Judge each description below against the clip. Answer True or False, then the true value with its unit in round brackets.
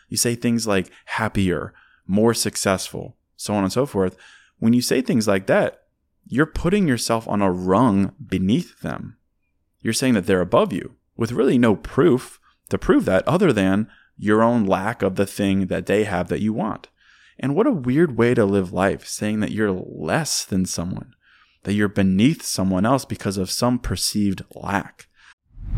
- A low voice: True (100 Hz)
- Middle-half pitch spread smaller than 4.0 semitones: True (3.5 semitones)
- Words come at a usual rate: True (180 wpm)